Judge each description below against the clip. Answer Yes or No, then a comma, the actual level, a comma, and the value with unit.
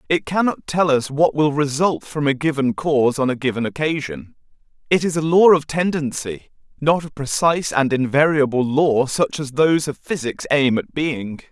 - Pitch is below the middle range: No, medium, 145 Hz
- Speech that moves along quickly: No, average, 180 wpm